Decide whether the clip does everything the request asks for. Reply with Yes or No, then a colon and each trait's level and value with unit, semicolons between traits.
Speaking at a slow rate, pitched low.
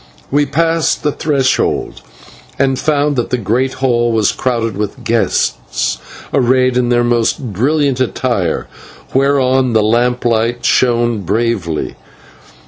Yes: slow, 120 wpm; low, 120 Hz